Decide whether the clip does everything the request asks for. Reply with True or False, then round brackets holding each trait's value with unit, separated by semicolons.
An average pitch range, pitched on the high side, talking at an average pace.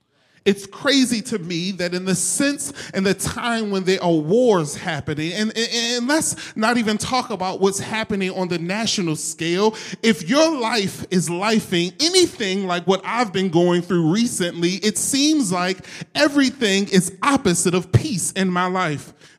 True (4.3 semitones; 195 Hz; 165 wpm)